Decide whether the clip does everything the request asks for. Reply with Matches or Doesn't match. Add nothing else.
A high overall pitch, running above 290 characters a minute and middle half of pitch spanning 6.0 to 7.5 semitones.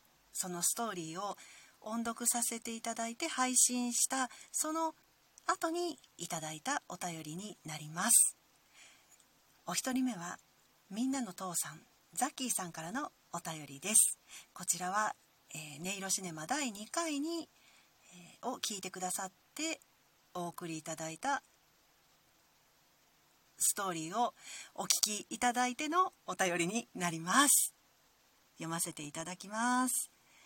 Doesn't match